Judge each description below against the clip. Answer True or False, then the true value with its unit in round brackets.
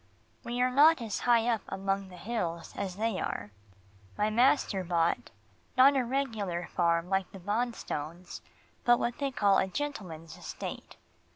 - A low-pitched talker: False (205 Hz)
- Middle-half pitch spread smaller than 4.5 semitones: False (5.2 semitones)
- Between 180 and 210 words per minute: False (155 wpm)